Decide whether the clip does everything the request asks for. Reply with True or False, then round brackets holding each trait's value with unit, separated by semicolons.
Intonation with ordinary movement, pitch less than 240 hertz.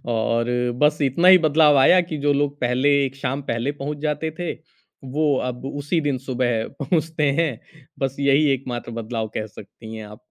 True (3.5 semitones; 140 Hz)